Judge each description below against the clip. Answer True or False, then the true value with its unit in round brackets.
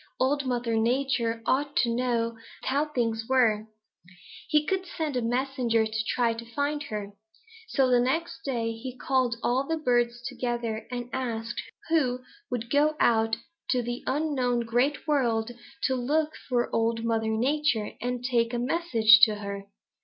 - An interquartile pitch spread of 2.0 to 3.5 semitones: True (2.9 semitones)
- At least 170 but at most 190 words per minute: False (155 wpm)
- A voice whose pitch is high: True (245 Hz)